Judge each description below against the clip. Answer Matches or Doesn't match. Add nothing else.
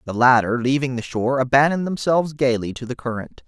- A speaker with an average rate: Matches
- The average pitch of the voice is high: Doesn't match